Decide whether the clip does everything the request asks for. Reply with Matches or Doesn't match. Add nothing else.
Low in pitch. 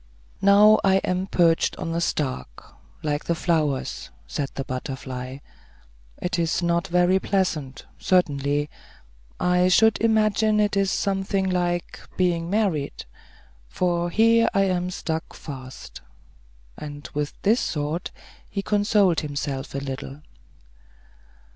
Doesn't match